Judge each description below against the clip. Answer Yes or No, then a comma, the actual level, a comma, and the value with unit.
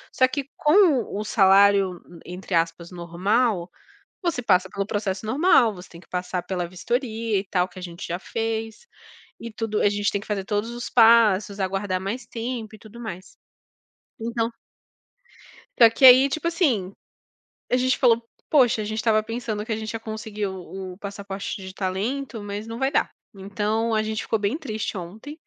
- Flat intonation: No, average, 3.4 semitones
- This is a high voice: Yes, high, 215 Hz